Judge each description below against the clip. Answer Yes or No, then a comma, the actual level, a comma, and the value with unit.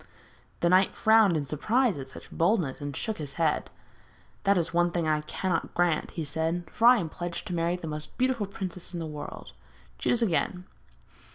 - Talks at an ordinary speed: Yes, average, 195 wpm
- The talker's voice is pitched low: No, medium, 175 Hz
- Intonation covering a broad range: No, average, 3.8 semitones